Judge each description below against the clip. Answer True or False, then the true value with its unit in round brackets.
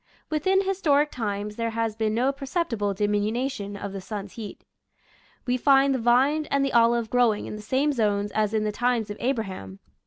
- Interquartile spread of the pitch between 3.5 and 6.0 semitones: True (4.6 semitones)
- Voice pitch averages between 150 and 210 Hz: False (230 Hz)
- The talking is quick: False (190 wpm)